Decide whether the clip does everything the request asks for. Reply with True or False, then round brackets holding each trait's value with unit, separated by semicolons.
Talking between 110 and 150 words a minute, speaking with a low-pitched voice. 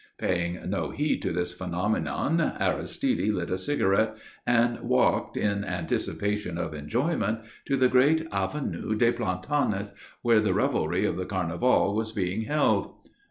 True (140 wpm; 105 Hz)